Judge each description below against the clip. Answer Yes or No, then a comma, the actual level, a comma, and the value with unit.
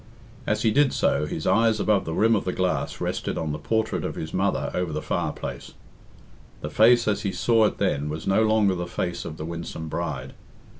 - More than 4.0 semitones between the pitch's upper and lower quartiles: Yes, wide, 5.6 semitones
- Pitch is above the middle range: No, very low, 95 Hz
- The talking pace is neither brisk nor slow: No, fast, 210 wpm